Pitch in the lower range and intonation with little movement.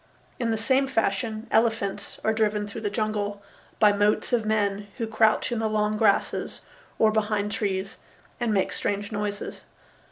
No: high, 215 Hz; narrow, 1.4 semitones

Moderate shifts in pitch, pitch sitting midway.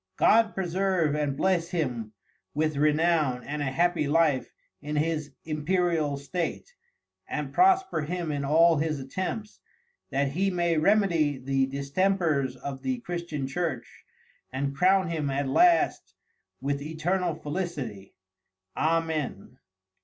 Yes: average, 4.0 semitones; medium, 155 Hz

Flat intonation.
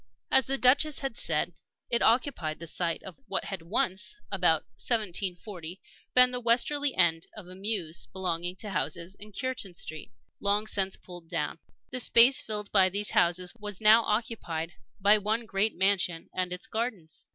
No: average, 4.2 semitones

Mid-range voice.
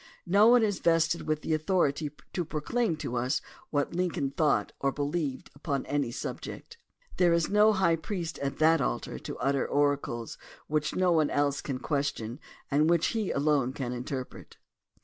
Yes: medium, 150 Hz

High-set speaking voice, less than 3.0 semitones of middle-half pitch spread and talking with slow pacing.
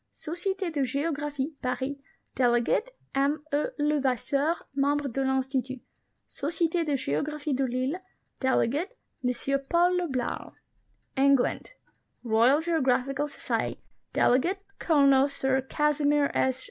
Yes: very high, 280 Hz; narrow, 2.6 semitones; slow, 110 wpm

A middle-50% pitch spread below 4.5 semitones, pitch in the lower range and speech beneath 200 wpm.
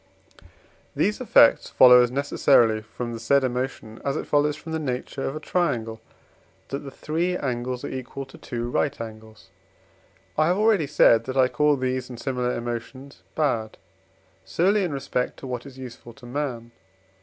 Yes: average, 3.3 semitones; low, 130 Hz; average, 170 wpm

